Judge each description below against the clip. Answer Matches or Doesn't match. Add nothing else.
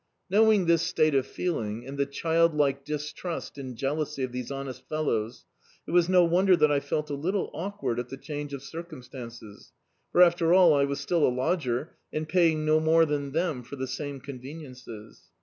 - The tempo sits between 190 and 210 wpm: Matches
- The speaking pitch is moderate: Matches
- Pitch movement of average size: Matches